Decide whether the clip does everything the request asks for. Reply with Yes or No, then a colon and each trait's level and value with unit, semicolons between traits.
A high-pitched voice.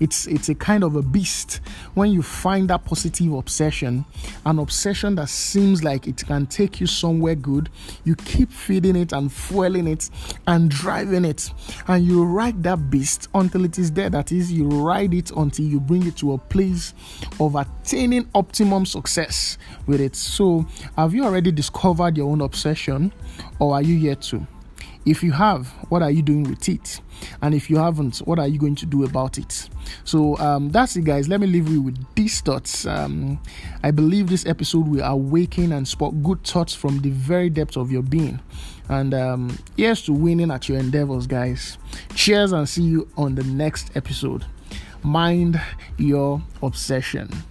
No: medium, 155 Hz